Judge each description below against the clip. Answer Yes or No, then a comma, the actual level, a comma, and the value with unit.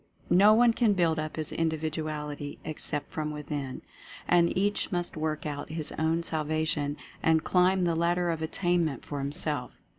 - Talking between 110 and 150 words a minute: No, average, 160 wpm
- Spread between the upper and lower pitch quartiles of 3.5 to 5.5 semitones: No, narrow, 2.6 semitones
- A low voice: No, medium, 160 Hz